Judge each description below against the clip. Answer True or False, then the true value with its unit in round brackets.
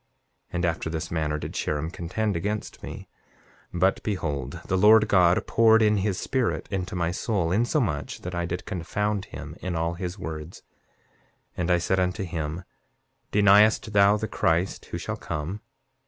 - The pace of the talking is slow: False (170 wpm)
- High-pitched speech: False (90 Hz)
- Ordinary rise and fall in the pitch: True (3.8 semitones)